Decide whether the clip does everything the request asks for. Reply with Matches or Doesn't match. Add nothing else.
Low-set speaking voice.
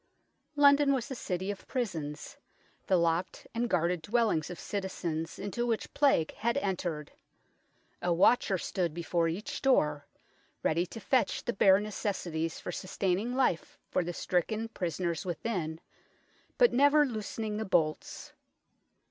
Doesn't match